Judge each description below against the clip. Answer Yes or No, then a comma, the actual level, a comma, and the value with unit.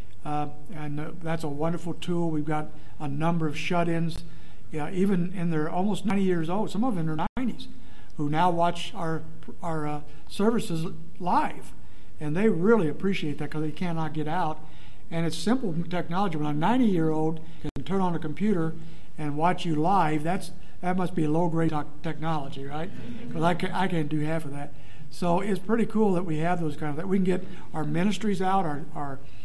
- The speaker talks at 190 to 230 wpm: Yes, average, 200 wpm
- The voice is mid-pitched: Yes, medium, 165 Hz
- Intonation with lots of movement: No, average, 3.1 semitones